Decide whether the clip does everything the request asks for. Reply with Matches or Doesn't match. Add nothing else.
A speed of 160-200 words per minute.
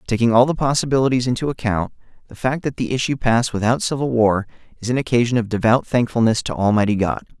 Matches